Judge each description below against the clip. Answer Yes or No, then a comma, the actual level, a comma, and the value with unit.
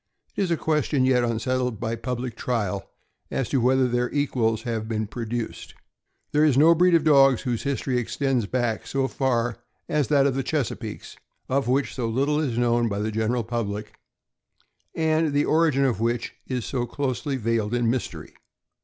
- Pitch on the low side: Yes, low, 125 Hz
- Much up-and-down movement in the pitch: No, average, 3.2 semitones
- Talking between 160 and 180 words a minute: Yes, average, 175 wpm